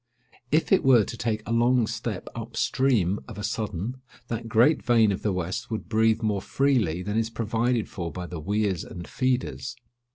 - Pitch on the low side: Yes, low, 110 Hz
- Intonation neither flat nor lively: Yes, average, 3.0 semitones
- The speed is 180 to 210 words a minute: Yes, average, 190 wpm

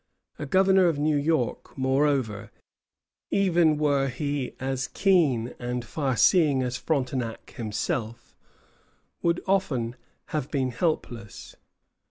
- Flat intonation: No, average, 4.2 semitones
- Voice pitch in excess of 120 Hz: Yes, low, 135 Hz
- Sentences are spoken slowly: Yes, slow, 110 wpm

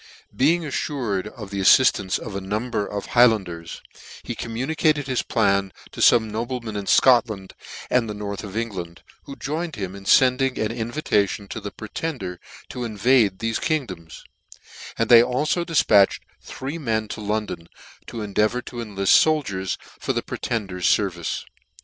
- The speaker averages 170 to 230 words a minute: No, average, 160 wpm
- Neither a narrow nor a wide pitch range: Yes, average, 4.3 semitones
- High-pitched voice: No, low, 110 Hz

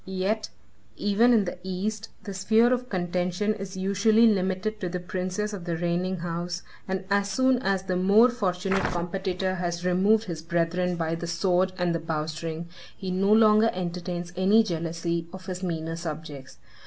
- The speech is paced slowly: No, average, 165 wpm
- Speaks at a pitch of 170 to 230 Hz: Yes, medium, 185 Hz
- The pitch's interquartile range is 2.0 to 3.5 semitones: Yes, average, 2.7 semitones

